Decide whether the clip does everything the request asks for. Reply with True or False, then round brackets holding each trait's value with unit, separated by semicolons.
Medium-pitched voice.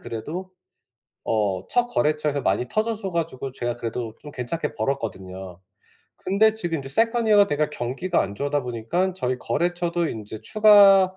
True (150 Hz)